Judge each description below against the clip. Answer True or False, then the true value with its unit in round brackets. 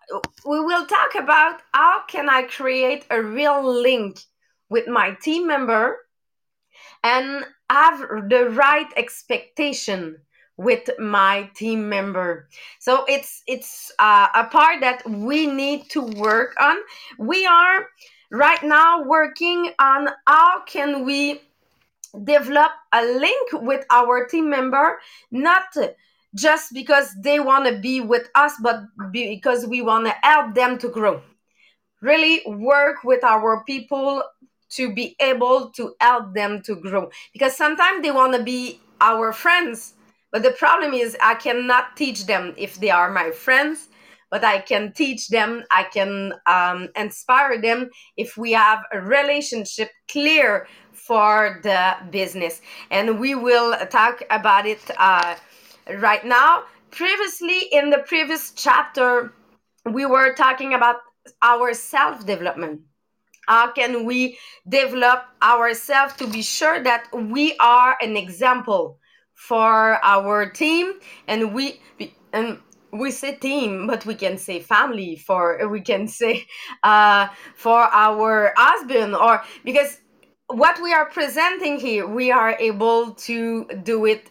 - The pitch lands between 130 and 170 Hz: False (250 Hz)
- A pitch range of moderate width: True (4.8 semitones)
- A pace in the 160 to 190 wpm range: False (135 wpm)